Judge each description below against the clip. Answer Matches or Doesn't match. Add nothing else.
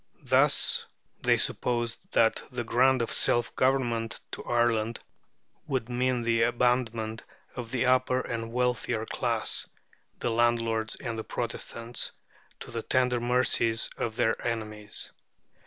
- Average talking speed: Doesn't match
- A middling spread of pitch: Doesn't match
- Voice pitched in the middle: Doesn't match